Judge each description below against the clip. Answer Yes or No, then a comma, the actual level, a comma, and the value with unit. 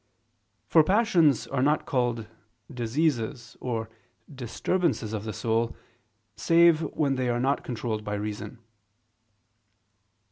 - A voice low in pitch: Yes, low, 125 Hz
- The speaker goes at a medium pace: No, slow, 110 wpm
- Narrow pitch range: No, average, 5.2 semitones